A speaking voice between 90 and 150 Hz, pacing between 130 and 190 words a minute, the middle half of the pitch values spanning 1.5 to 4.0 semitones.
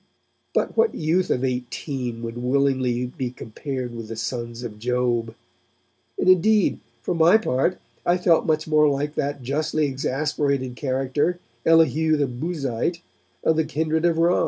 No: medium, 140 Hz; average, 150 wpm; average, 4.4 semitones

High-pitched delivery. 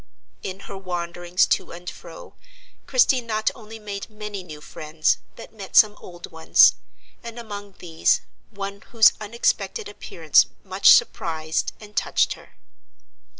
Yes: high, 200 Hz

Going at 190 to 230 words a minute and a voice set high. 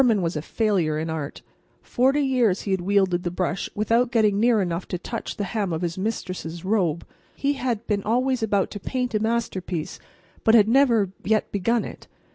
Yes: average, 195 wpm; high, 205 Hz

